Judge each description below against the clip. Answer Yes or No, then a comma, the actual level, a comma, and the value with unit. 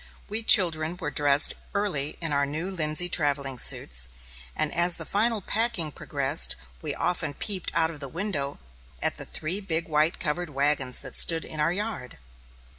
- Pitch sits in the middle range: Yes, medium, 160 Hz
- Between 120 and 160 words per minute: No, average, 170 wpm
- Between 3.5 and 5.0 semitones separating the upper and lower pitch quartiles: Yes, average, 3.8 semitones